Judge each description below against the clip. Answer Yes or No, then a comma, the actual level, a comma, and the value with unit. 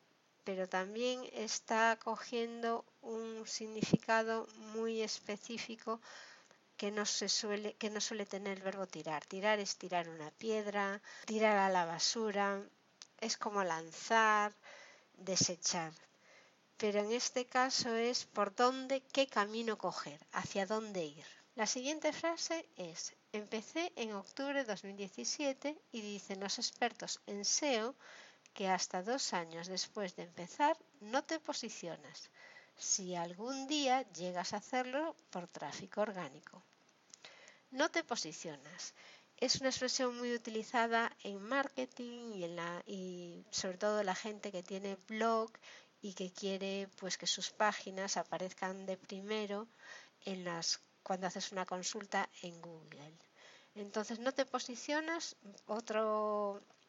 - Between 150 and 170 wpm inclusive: No, average, 130 wpm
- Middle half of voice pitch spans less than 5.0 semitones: Yes, average, 3.8 semitones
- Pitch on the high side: Yes, high, 210 Hz